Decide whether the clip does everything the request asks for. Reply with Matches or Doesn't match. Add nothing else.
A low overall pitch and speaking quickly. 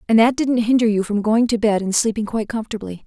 Doesn't match